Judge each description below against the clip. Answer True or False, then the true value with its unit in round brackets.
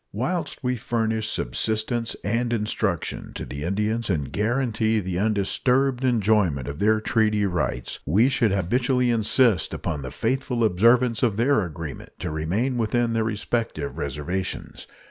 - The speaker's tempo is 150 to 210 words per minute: False (140 wpm)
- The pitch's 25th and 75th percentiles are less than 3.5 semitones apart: False (4.1 semitones)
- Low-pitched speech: True (110 Hz)